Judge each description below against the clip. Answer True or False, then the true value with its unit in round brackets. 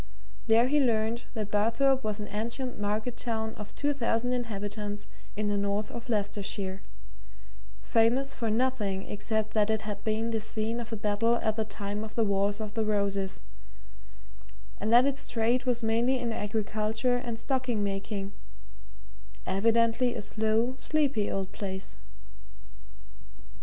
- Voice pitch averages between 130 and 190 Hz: False (220 Hz)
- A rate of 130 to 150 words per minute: True (145 wpm)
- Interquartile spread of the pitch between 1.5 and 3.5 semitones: True (2.4 semitones)